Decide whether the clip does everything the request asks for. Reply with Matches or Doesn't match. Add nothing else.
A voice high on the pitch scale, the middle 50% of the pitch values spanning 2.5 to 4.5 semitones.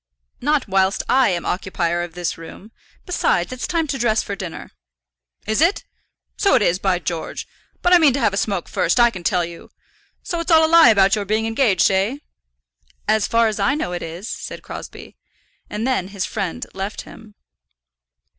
Doesn't match